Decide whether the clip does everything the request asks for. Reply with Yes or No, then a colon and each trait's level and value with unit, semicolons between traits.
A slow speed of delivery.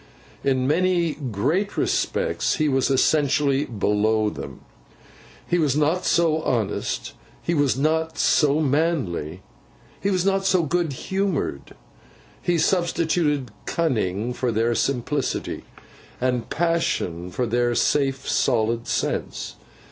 Yes: slow, 115 wpm